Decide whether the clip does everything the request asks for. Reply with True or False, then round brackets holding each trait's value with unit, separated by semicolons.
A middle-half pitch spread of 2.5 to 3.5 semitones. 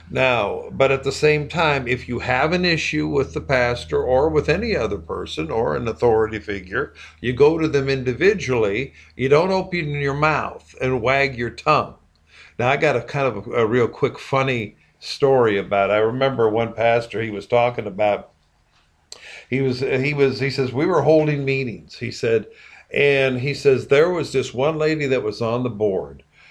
False (3.9 semitones)